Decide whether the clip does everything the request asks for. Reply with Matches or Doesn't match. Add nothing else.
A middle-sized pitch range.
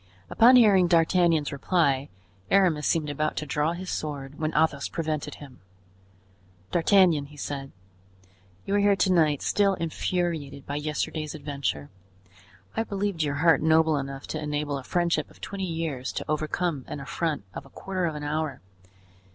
Matches